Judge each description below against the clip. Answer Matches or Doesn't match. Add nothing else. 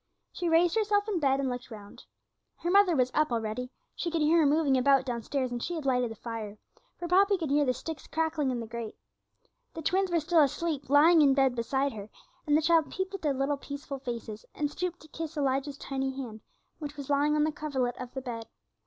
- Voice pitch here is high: Matches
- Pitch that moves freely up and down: Doesn't match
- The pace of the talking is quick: Matches